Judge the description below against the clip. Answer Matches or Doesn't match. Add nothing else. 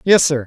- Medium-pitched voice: Matches